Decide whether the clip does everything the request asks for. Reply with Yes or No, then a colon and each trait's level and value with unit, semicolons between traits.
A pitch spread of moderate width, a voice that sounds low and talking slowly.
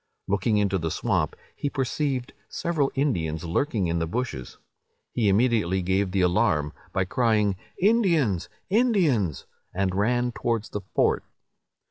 No: wide, 6.0 semitones; low, 105 Hz; slow, 130 wpm